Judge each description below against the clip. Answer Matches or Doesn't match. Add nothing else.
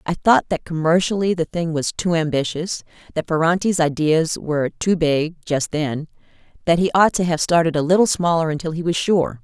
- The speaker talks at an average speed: Matches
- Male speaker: Doesn't match